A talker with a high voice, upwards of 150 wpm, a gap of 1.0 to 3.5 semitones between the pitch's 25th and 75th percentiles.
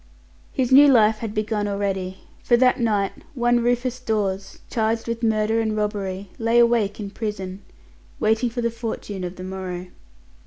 Yes: high, 215 Hz; average, 160 wpm; average, 2.9 semitones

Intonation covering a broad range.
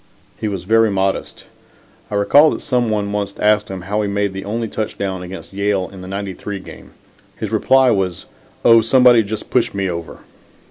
No: narrow, 2.5 semitones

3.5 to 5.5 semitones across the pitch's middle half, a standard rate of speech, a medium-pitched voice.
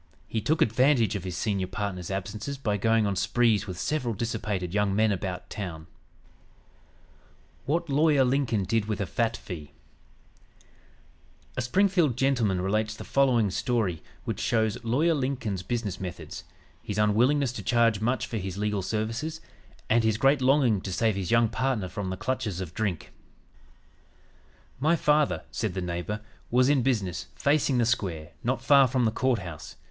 No: average, 4.8 semitones; average, 160 wpm; low, 110 Hz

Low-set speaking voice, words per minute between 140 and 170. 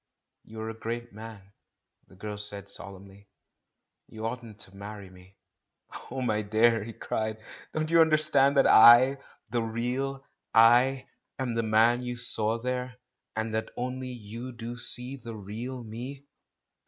Yes: low, 115 Hz; average, 160 wpm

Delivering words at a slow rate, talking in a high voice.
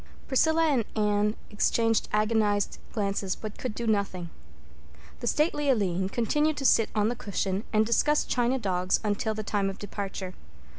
No: average, 155 wpm; high, 215 Hz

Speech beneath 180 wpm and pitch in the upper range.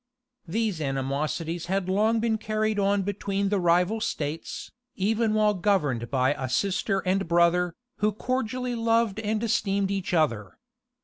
Yes: average, 140 wpm; high, 195 Hz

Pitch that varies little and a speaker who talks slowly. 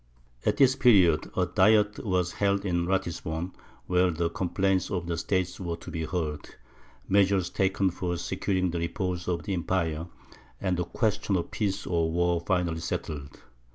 No: narrow, 2.3 semitones; average, 160 wpm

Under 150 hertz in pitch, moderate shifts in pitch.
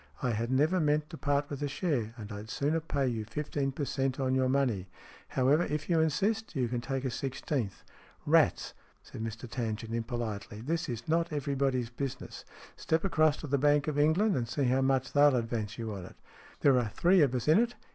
Yes: low, 135 Hz; average, 4.1 semitones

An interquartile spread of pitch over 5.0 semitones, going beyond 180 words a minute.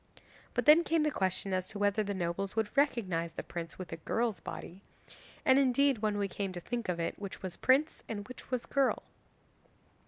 Yes: wide, 5.5 semitones; fast, 205 wpm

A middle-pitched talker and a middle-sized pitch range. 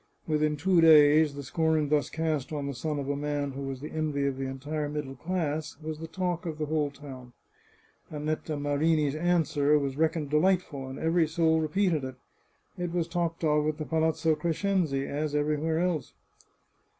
No: medium, 155 Hz; narrow, 2.1 semitones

